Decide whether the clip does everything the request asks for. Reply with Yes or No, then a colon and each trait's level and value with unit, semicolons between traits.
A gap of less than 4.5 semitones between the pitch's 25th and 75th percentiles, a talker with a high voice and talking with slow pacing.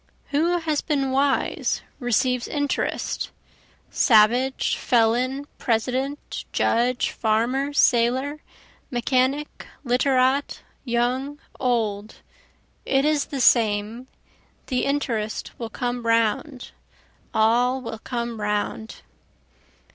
Yes: average, 3.1 semitones; very high, 250 Hz; slow, 85 wpm